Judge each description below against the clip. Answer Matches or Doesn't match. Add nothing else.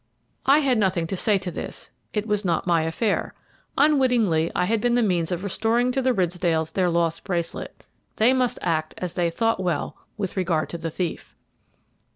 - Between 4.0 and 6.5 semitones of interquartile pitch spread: Matches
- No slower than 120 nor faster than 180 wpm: Doesn't match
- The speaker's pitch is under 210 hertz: Matches